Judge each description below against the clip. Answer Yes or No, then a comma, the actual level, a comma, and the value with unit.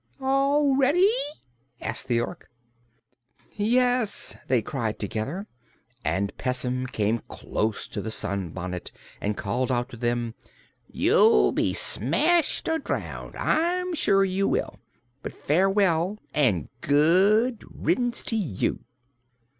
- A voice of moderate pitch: Yes, medium, 150 Hz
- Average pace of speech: No, slow, 115 wpm